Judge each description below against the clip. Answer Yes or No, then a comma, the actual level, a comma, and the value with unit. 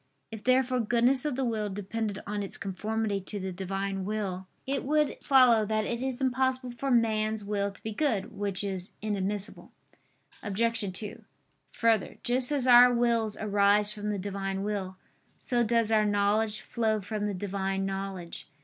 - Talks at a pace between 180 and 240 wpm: No, average, 165 wpm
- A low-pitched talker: No, high, 210 Hz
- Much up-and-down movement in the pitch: No, average, 3.1 semitones